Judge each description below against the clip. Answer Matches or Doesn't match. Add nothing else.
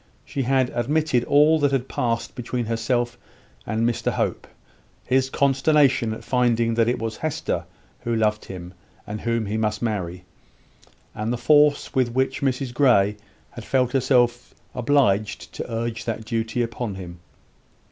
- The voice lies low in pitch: Matches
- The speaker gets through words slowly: Doesn't match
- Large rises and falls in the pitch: Doesn't match